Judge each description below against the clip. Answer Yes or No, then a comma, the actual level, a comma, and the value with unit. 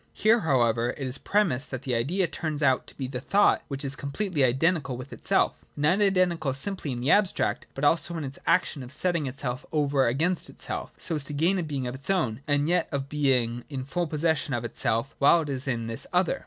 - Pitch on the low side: No, medium, 145 Hz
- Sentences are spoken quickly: Yes, fast, 225 wpm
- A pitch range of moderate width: Yes, average, 4.6 semitones